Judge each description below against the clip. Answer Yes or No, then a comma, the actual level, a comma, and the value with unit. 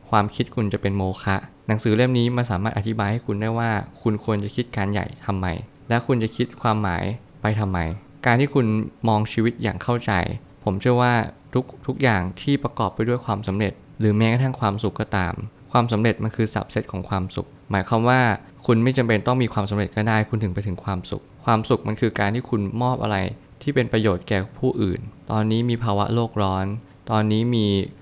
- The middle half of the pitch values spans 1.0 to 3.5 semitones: Yes, average, 3.0 semitones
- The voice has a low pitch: Yes, low, 110 Hz